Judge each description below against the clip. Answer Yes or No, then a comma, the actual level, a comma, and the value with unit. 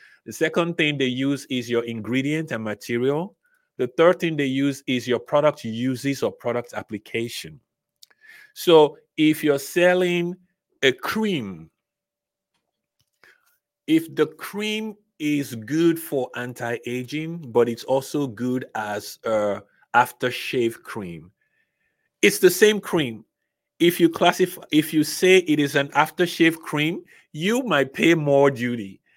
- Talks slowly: Yes, slow, 130 wpm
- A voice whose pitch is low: No, medium, 150 Hz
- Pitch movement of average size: No, wide, 5.8 semitones